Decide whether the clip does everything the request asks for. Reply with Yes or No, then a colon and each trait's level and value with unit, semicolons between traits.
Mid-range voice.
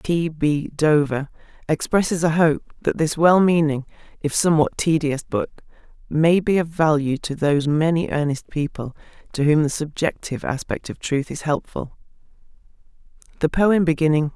Yes: medium, 155 Hz